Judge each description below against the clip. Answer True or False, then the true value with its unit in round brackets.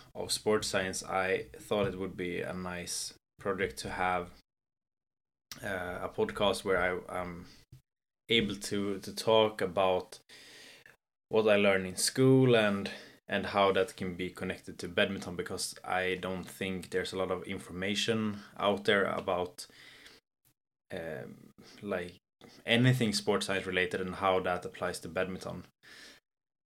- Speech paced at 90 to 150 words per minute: True (140 wpm)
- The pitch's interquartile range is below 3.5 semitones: True (2.4 semitones)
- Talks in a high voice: False (95 Hz)